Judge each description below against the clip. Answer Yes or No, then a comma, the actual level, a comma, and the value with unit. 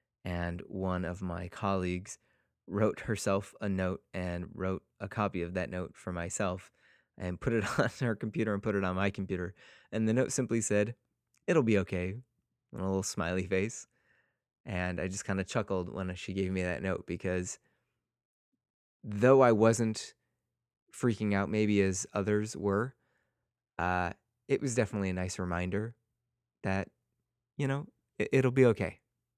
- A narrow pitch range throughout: No, average, 3.5 semitones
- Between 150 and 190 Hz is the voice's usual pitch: No, low, 100 Hz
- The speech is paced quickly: No, average, 160 wpm